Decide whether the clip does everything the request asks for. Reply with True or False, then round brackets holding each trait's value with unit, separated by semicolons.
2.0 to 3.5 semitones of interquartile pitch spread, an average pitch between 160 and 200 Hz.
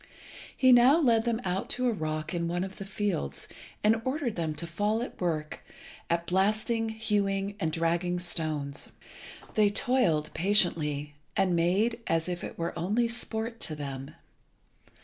False (5.2 semitones; 190 Hz)